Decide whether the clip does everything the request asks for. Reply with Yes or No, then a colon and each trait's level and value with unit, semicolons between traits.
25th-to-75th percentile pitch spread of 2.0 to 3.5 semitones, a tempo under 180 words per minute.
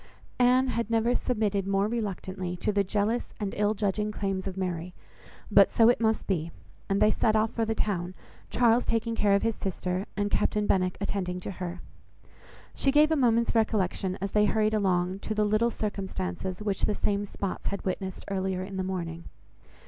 No: average, 2.7 semitones; average, 185 wpm